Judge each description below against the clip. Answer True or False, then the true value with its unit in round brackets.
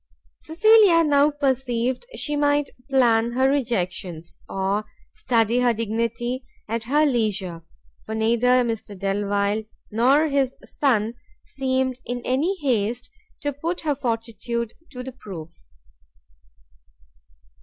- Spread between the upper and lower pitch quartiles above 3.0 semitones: True (4.0 semitones)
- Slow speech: True (110 wpm)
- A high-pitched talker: True (245 Hz)